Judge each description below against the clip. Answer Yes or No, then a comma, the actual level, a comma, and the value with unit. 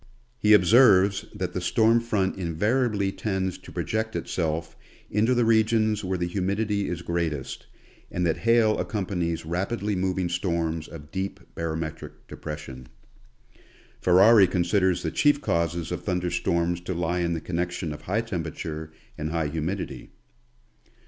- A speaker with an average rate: Yes, average, 145 wpm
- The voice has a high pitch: No, very low, 90 Hz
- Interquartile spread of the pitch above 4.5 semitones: No, average, 3.7 semitones